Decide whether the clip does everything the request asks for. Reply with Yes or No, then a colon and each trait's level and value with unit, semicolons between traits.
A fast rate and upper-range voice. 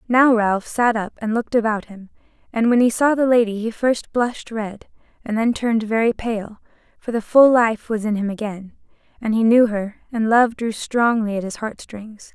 Yes: fast, 210 wpm; high, 225 Hz